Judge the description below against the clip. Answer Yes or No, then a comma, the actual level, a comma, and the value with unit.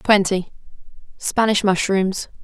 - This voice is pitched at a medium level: No, high, 195 Hz